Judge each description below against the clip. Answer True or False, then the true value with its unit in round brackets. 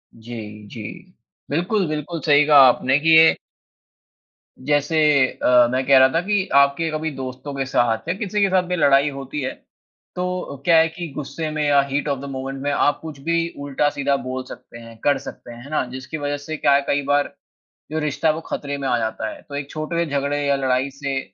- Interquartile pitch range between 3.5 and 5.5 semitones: False (2.9 semitones)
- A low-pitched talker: False (145 Hz)